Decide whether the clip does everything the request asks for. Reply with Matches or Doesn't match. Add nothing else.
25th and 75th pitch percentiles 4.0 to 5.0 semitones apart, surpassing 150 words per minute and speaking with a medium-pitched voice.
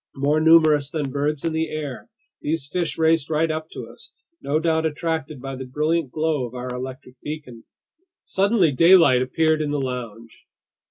Doesn't match